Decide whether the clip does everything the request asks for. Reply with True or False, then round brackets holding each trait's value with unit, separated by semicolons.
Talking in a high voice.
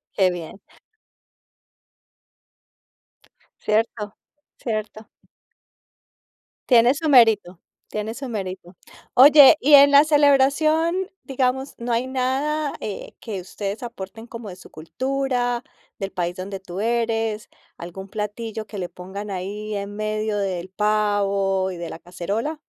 True (215 Hz)